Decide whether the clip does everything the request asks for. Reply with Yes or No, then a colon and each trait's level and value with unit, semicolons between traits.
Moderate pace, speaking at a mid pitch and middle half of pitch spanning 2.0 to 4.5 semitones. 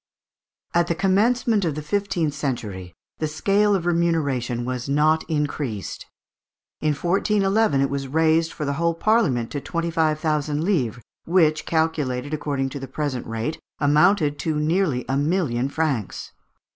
Yes: average, 145 wpm; medium, 155 Hz; average, 3.7 semitones